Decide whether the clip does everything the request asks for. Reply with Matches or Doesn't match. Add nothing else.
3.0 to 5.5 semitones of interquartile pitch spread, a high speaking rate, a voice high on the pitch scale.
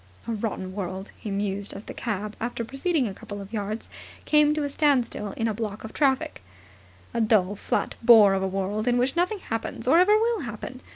Matches